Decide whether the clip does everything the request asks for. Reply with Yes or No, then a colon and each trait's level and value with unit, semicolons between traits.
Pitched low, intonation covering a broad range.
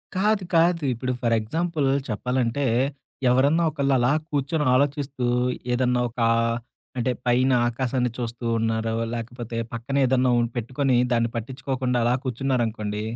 No: low, 125 Hz; average, 2.7 semitones